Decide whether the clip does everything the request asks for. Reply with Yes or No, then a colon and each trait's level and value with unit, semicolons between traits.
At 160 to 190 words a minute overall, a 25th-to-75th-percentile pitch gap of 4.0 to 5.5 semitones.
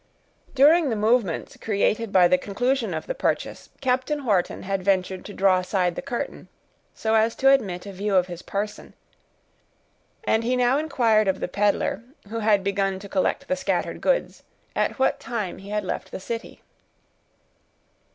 Yes: average, 170 wpm; average, 4.4 semitones